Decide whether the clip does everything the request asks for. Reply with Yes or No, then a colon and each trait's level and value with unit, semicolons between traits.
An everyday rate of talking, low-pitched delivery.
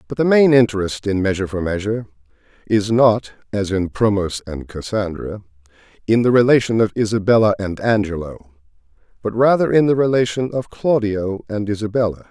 Yes: average, 150 wpm; low, 110 Hz